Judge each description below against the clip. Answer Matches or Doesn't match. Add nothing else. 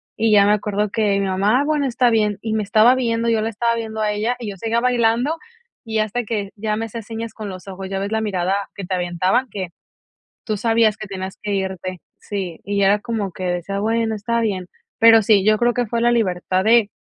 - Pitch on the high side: Matches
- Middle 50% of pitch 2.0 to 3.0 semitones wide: Matches